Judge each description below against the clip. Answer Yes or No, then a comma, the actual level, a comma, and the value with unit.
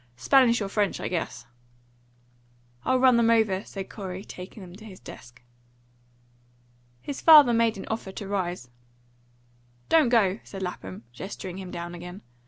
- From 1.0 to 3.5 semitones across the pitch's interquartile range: No, average, 4.3 semitones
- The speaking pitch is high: Yes, high, 195 Hz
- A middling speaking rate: Yes, average, 150 wpm